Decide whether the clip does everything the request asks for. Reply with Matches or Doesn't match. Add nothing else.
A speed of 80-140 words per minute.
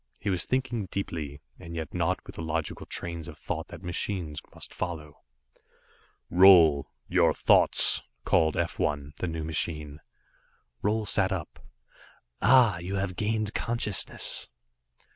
Matches